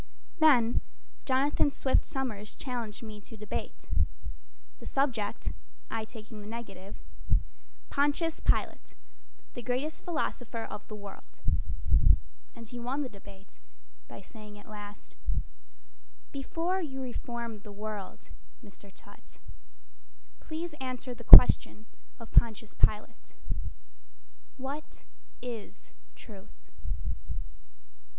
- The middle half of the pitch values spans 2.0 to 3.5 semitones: No, average, 4.1 semitones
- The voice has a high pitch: Yes, high, 230 Hz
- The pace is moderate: No, slow, 100 wpm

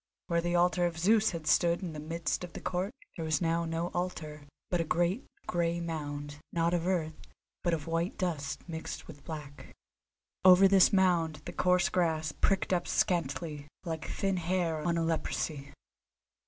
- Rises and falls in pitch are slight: Yes, narrow, 2.1 semitones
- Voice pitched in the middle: Yes, medium, 170 Hz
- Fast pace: No, average, 175 wpm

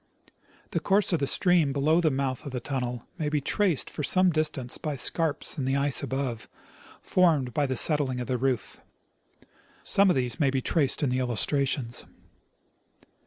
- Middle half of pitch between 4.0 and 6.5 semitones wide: No, average, 3.3 semitones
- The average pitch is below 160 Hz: Yes, medium, 140 Hz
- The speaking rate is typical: Yes, average, 175 wpm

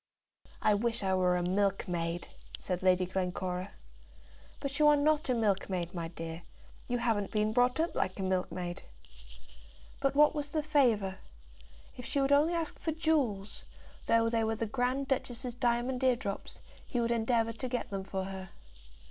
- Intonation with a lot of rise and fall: Yes, wide, 5.7 semitones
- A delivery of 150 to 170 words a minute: Yes, average, 165 wpm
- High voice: Yes, high, 225 Hz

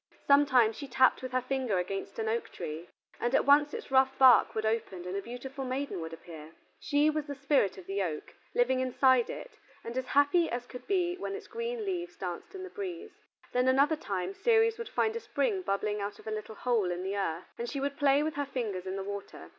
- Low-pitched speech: No, very high, 255 Hz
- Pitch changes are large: Yes, wide, 6.4 semitones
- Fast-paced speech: Yes, fast, 230 wpm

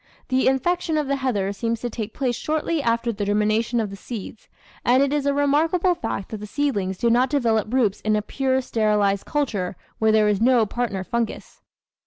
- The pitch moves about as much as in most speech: Yes, average, 4.6 semitones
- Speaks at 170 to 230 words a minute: Yes, average, 200 wpm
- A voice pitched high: Yes, high, 235 Hz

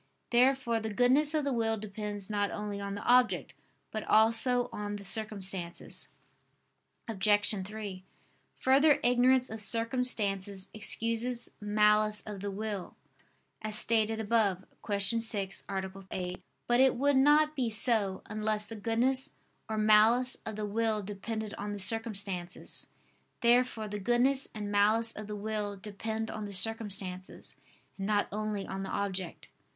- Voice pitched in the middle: No, high, 215 Hz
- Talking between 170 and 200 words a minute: No, average, 145 wpm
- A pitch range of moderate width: No, narrow, 2.3 semitones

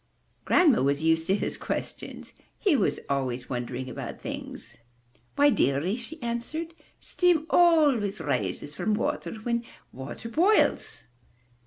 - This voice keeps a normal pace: No, slow, 130 wpm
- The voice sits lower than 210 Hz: No, high, 220 Hz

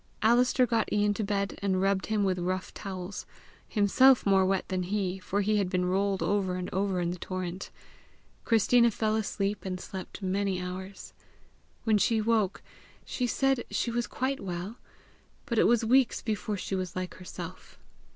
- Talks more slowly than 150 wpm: No, average, 170 wpm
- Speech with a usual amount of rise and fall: Yes, average, 3.0 semitones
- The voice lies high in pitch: Yes, high, 200 Hz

